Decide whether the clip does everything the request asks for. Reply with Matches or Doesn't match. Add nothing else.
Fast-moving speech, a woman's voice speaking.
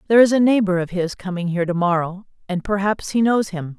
Matches